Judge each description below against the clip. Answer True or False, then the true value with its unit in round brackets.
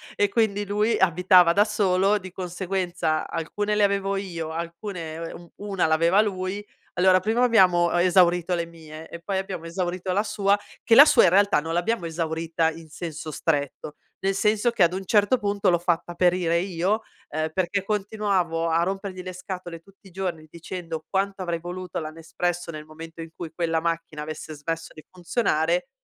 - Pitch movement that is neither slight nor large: True (3.0 semitones)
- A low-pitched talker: False (180 Hz)